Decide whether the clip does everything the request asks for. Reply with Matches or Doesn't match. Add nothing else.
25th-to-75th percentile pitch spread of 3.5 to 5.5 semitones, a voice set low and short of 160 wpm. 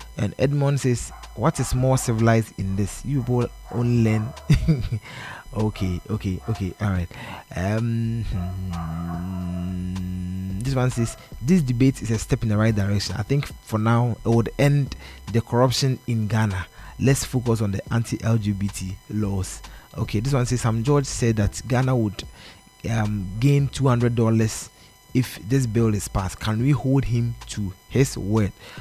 Matches